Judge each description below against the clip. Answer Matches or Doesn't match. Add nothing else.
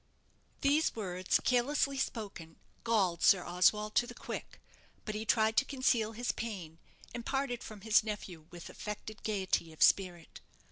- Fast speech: Doesn't match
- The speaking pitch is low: Doesn't match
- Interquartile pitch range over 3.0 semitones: Matches